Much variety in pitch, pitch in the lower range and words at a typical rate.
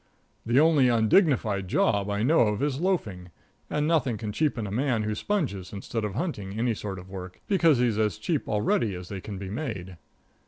Yes: wide, 6.0 semitones; low, 110 Hz; average, 195 wpm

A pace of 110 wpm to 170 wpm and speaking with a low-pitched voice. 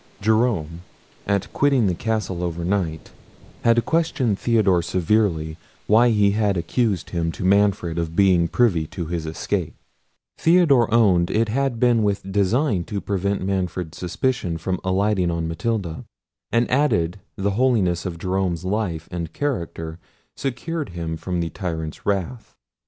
Yes: average, 140 wpm; very low, 95 Hz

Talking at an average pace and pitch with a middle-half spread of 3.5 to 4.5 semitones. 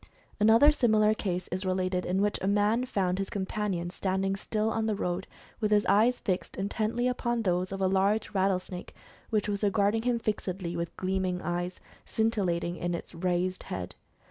No: average, 175 wpm; average, 2.8 semitones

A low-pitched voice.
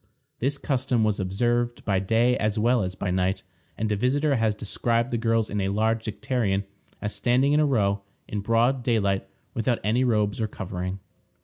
Yes: low, 110 Hz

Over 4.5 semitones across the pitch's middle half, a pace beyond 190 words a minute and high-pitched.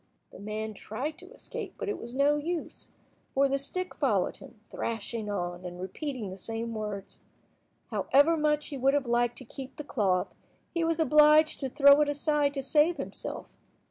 No: wide, 5.4 semitones; average, 180 wpm; very high, 275 Hz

